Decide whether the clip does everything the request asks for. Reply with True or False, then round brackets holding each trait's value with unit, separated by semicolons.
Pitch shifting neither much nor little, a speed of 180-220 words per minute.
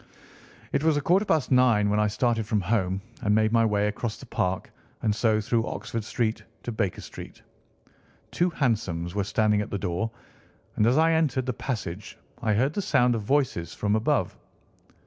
True (3.6 semitones; 185 wpm)